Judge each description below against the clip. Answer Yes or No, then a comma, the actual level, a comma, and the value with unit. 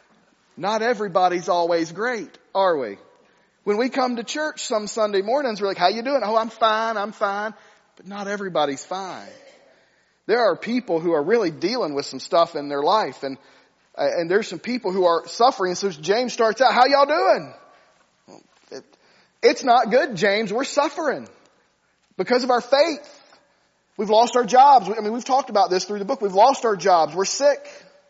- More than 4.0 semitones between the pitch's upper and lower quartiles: Yes, average, 5.0 semitones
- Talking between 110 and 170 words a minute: No, average, 190 wpm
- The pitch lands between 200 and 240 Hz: Yes, high, 210 Hz